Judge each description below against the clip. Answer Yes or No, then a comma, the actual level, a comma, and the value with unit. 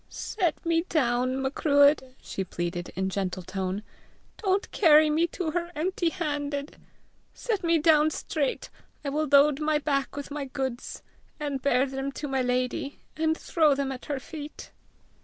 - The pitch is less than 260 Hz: No, very high, 285 Hz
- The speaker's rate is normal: Yes, average, 160 wpm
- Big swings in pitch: No, average, 3.1 semitones